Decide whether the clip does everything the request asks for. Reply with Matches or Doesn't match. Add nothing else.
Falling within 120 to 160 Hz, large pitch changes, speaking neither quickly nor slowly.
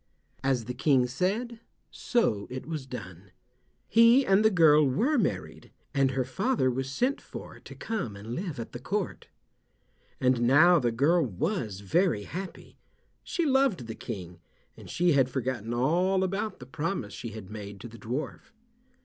Matches